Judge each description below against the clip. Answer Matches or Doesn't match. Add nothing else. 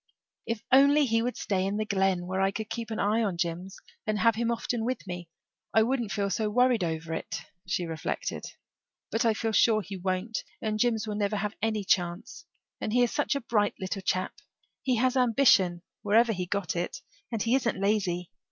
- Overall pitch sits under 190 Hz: Doesn't match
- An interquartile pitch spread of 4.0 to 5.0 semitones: Doesn't match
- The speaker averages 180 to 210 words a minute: Matches